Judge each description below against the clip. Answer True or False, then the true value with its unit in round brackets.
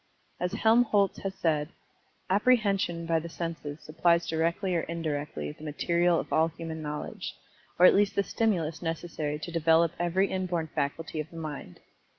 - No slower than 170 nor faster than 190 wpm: False (160 wpm)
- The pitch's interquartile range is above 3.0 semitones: False (2.6 semitones)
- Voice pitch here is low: False (165 Hz)